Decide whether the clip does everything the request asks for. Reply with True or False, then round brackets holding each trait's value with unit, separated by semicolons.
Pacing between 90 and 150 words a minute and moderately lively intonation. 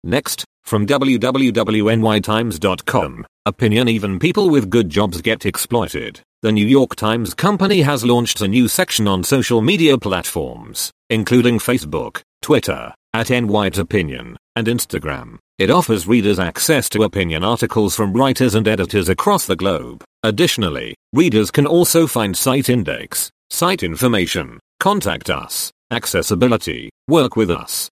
True (135 wpm; 3.3 semitones)